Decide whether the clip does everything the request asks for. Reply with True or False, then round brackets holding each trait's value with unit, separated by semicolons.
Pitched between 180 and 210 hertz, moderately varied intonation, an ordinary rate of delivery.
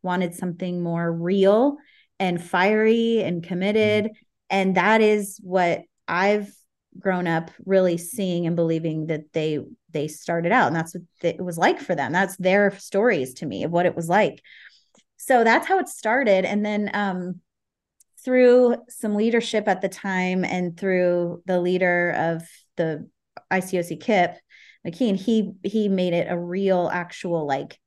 True (185 Hz; 3.4 semitones; 155 wpm)